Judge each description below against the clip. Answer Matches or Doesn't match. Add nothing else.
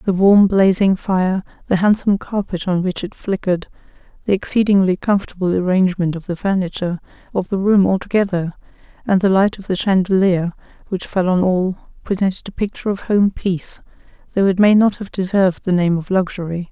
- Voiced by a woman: Matches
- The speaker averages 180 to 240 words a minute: Doesn't match